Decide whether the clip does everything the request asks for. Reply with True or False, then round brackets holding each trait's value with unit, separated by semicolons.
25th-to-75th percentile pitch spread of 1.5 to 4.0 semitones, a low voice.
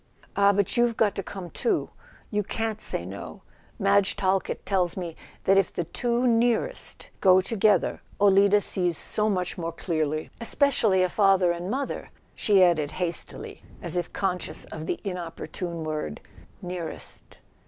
False (3.1 semitones; 190 Hz)